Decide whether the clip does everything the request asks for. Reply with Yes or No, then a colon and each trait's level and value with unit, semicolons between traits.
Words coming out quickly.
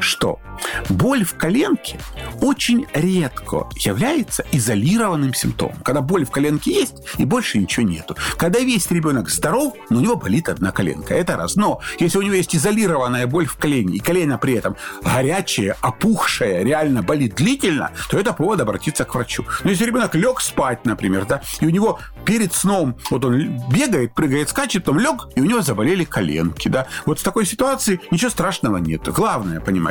Yes: fast, 175 wpm